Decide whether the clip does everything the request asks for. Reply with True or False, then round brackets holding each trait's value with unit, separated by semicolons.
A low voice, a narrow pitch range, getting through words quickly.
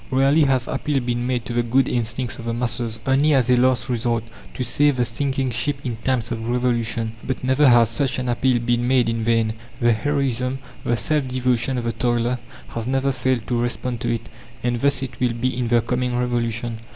True (125 Hz; 1.8 semitones; 210 wpm)